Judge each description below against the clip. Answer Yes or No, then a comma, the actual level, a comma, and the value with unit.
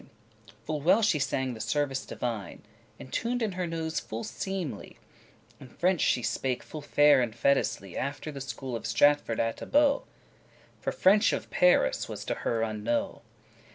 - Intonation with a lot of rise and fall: Yes, wide, 6.9 semitones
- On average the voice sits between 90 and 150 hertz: Yes, medium, 140 Hz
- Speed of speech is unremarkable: Yes, average, 165 wpm